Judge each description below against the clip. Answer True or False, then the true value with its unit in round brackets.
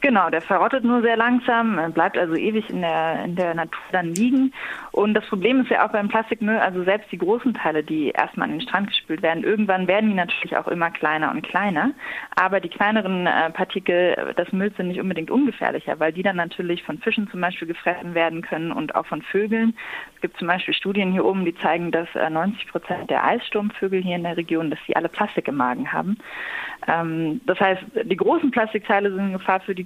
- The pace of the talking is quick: True (210 wpm)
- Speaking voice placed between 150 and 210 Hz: True (190 Hz)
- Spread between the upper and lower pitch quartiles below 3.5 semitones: False (4.0 semitones)